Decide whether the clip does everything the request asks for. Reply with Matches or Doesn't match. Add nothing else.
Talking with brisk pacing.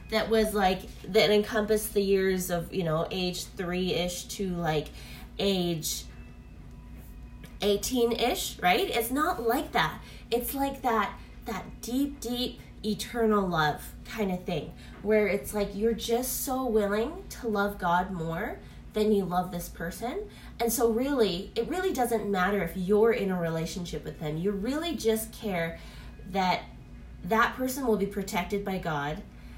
Doesn't match